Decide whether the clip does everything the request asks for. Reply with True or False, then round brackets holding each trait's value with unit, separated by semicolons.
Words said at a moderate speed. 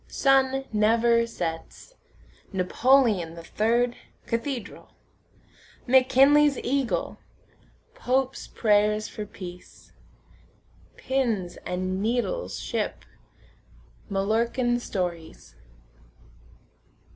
False (65 wpm)